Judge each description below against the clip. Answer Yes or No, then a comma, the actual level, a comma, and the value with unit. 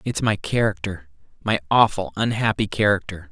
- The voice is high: No, low, 100 Hz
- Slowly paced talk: Yes, slow, 125 wpm